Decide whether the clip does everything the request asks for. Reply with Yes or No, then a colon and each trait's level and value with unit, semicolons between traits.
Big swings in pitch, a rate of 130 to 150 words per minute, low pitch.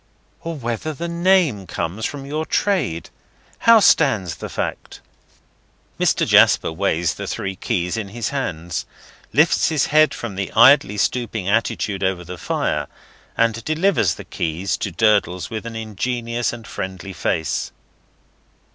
Yes: wide, 7.0 semitones; average, 140 wpm; low, 110 Hz